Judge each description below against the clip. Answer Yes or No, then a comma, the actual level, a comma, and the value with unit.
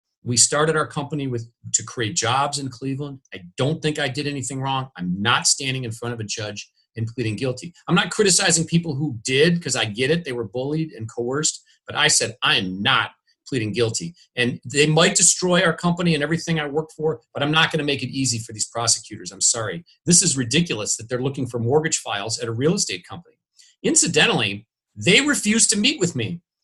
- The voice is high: No, medium, 140 Hz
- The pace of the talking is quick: Yes, fast, 215 wpm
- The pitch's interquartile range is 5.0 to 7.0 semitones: Yes, average, 5.3 semitones